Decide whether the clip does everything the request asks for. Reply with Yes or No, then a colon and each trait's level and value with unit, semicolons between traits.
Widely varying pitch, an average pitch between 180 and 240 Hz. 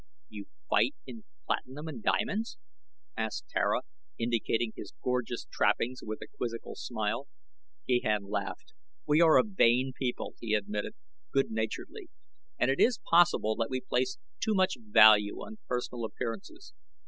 No: wide, 6.6 semitones; low, 125 Hz